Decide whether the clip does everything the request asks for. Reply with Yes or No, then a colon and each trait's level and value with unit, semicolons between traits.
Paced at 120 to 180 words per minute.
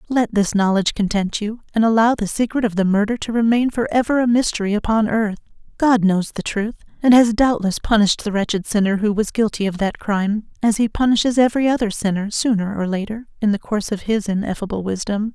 No: fast, 205 wpm